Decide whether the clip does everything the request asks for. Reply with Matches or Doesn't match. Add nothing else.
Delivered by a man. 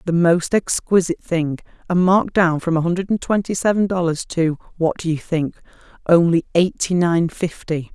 Doesn't match